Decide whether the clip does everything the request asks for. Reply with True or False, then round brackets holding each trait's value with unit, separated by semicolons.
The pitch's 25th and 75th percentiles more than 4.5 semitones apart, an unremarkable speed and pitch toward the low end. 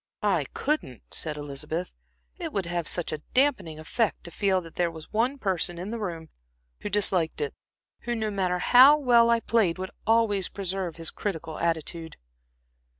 False (5.4 semitones; 170 wpm; 185 Hz)